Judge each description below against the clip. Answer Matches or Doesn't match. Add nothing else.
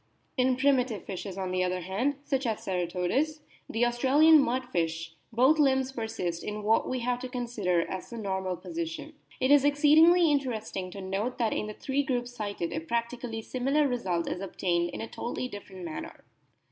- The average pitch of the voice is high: Matches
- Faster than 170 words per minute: Matches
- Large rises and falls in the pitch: Matches